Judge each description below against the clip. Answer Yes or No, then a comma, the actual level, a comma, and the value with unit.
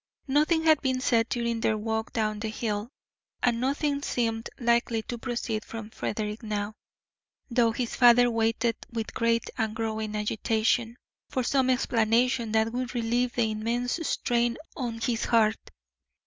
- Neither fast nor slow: Yes, average, 150 wpm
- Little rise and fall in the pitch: Yes, narrow, 1.7 semitones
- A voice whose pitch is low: No, high, 230 Hz